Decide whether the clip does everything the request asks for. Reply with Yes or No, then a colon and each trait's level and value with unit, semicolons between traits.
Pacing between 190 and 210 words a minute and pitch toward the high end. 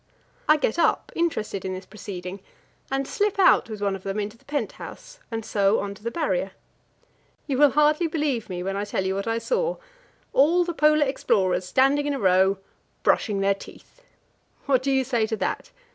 Yes: average, 200 wpm; high, 230 Hz